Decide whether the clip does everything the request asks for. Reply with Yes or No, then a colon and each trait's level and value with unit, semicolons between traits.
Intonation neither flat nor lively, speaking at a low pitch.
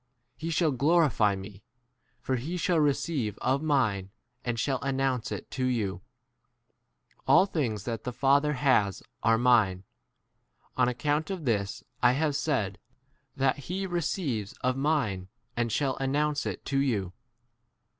Yes: average, 5.0 semitones; low, 130 Hz